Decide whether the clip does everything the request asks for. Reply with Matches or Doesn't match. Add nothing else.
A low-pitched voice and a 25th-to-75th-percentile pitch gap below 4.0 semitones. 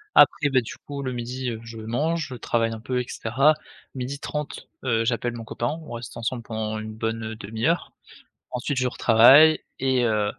Matches